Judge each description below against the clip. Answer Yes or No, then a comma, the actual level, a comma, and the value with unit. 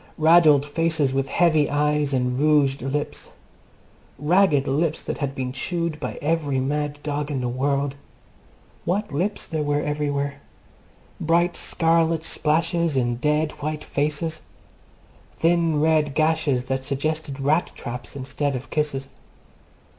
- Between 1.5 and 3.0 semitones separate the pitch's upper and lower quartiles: Yes, narrow, 2.6 semitones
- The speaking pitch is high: No, medium, 150 Hz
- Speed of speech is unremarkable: No, slow, 130 wpm